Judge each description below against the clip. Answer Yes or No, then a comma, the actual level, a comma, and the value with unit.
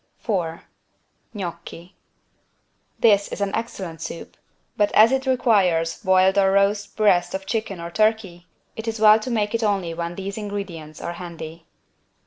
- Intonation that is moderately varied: Yes, average, 3.8 semitones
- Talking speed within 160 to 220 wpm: No, average, 150 wpm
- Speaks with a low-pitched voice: No, high, 195 Hz